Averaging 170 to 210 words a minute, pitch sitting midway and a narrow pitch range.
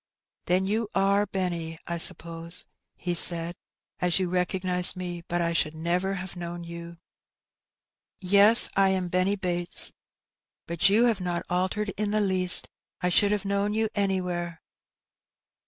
No: average, 145 wpm; medium, 180 Hz; narrow, 2.3 semitones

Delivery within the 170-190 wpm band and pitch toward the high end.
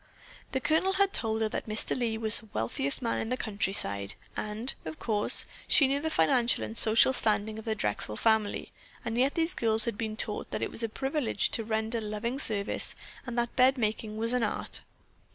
No: fast, 205 wpm; high, 225 Hz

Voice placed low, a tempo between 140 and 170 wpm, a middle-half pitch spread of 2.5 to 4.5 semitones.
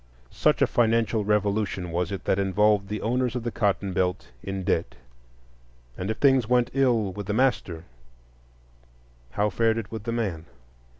Yes: low, 105 Hz; average, 165 wpm; average, 3.2 semitones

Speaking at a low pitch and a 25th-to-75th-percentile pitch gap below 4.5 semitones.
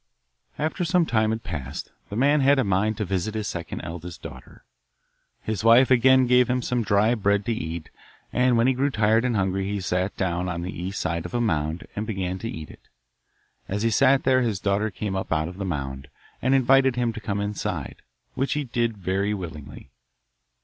No: low, 105 Hz; average, 5.1 semitones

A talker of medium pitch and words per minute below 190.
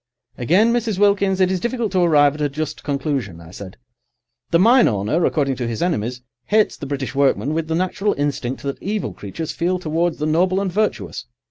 No: medium, 160 Hz; average, 200 wpm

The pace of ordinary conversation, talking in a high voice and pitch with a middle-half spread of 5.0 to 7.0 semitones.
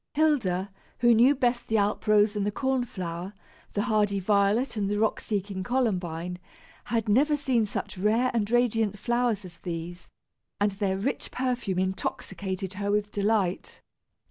No: average, 155 wpm; high, 205 Hz; average, 3.8 semitones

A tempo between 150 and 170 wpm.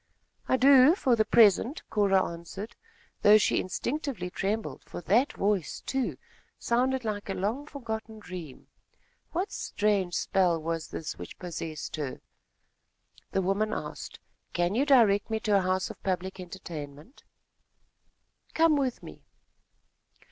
No: slow, 135 wpm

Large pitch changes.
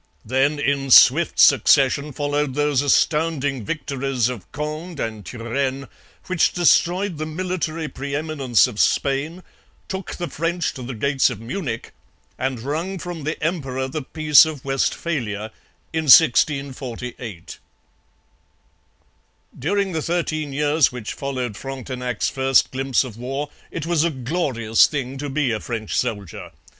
No: average, 3.7 semitones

